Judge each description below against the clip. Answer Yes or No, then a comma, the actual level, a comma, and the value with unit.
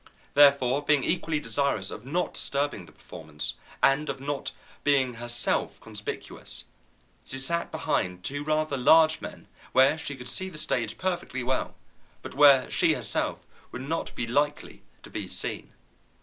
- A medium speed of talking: Yes, average, 150 wpm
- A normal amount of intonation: Yes, average, 3.2 semitones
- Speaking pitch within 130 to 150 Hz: Yes, medium, 140 Hz